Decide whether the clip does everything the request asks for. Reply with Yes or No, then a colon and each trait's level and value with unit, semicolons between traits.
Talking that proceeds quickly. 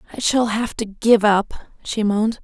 No: average, 195 wpm